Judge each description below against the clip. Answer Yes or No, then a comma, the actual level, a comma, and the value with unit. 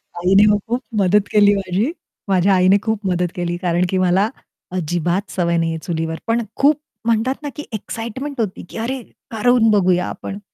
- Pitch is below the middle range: No, high, 195 Hz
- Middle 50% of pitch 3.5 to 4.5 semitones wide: Yes, average, 4.0 semitones